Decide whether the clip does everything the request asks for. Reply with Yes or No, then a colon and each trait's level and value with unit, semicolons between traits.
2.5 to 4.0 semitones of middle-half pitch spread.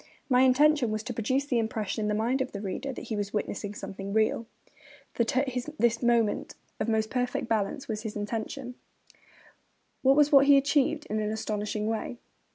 Yes: average, 3.5 semitones